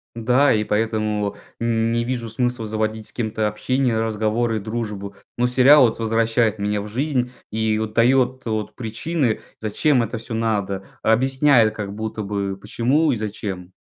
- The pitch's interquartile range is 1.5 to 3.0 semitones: Yes, narrow, 2.4 semitones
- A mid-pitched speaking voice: No, low, 110 Hz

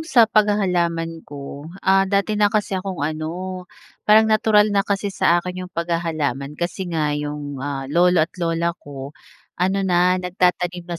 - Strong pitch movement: No, average, 3.5 semitones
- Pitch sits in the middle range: Yes, medium, 175 Hz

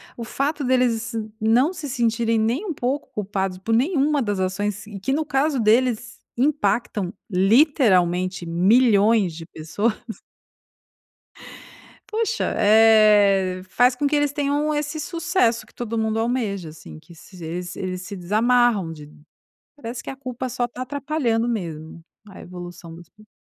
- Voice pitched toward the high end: Yes, high, 225 Hz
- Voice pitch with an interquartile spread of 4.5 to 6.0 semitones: Yes, wide, 5.5 semitones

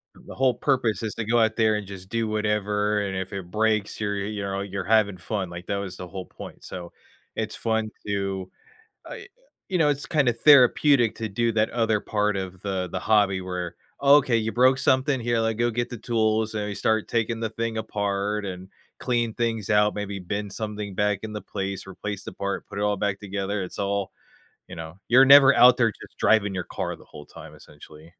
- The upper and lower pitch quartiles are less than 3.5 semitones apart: Yes, average, 2.7 semitones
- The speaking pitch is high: No, low, 105 Hz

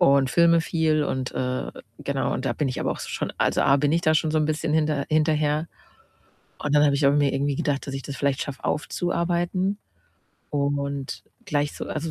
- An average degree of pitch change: No, narrow, 2.0 semitones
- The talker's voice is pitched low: No, medium, 150 Hz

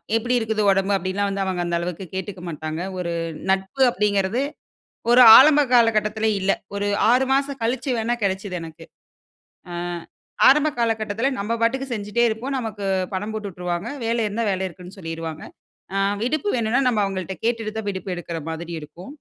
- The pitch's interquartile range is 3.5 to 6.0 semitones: Yes, average, 3.8 semitones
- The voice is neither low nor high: No, high, 205 Hz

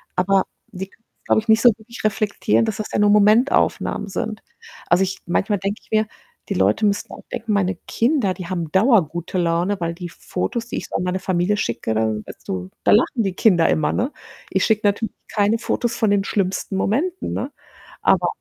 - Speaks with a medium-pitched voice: No, high, 200 Hz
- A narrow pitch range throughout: No, average, 3.2 semitones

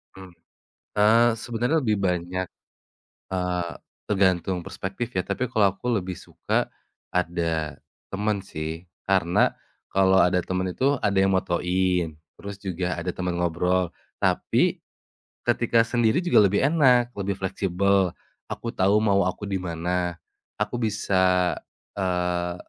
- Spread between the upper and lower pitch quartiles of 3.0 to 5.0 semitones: No, narrow, 2.6 semitones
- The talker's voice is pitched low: Yes, very low, 95 Hz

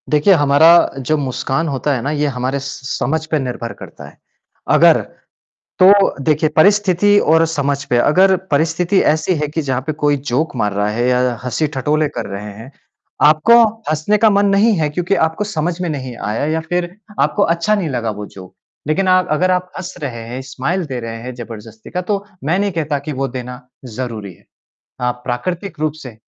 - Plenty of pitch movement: Yes, wide, 5.7 semitones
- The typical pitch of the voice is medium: Yes, medium, 150 Hz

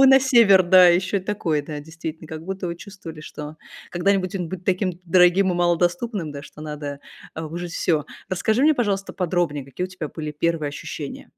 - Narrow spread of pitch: No, average, 3.5 semitones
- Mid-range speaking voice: Yes, medium, 175 Hz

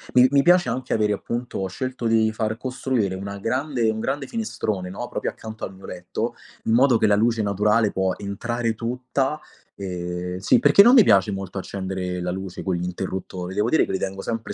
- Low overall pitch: Yes, low, 110 Hz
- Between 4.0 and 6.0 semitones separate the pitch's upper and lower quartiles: Yes, average, 4.3 semitones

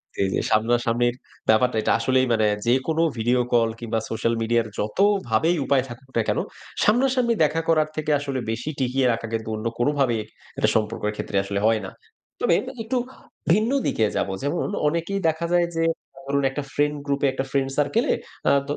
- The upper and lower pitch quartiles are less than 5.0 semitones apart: No, wide, 5.4 semitones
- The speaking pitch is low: Yes, low, 130 Hz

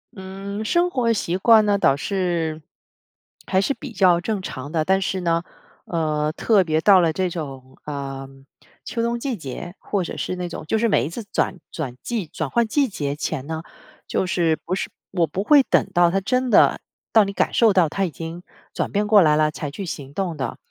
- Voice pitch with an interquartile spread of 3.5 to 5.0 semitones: Yes, average, 4.6 semitones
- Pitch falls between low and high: Yes, medium, 180 Hz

